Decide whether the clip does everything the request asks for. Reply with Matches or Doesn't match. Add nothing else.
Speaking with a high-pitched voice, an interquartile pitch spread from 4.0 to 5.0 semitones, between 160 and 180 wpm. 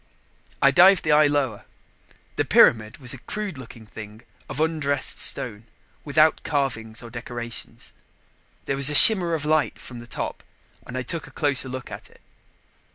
Doesn't match